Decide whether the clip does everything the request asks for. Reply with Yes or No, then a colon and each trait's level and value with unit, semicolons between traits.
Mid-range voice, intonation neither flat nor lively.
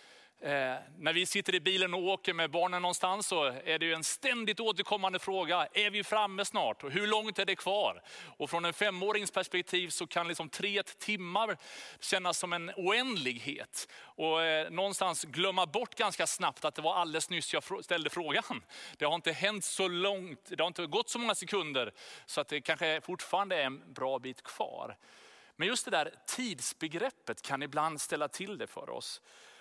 Yes: medium, 180 Hz; average, 3.7 semitones